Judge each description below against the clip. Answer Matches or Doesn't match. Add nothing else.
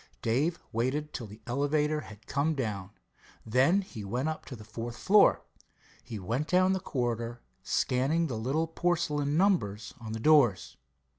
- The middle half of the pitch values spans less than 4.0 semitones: Doesn't match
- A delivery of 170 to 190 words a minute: Doesn't match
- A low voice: Matches